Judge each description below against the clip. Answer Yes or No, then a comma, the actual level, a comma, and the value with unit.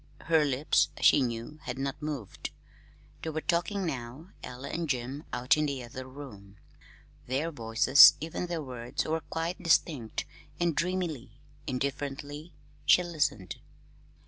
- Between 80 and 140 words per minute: Yes, slow, 135 wpm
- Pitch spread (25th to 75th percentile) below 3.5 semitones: No, average, 4.3 semitones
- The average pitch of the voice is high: No, medium, 140 Hz